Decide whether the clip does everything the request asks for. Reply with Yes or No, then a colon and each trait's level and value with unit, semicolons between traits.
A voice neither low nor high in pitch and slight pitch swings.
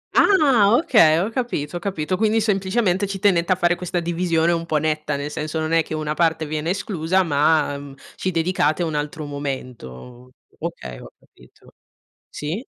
No: medium, 165 Hz; average, 3.9 semitones